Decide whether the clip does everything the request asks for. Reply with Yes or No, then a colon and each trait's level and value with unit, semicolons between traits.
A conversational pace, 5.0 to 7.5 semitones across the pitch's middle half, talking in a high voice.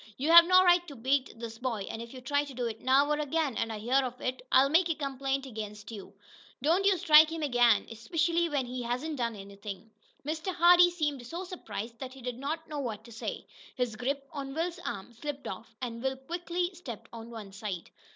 No: fast, 220 wpm; wide, 5.5 semitones; very high, 265 Hz